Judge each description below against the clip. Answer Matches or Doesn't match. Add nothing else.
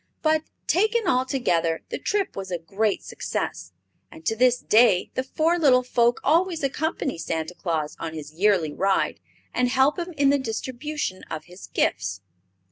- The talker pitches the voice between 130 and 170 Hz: Doesn't match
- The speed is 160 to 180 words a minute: Matches